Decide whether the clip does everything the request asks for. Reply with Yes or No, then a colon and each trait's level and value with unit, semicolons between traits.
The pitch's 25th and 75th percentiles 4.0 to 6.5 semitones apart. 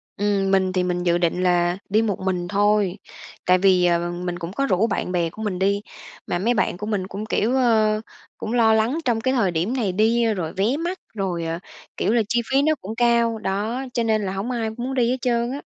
Yes: average, 4.3 semitones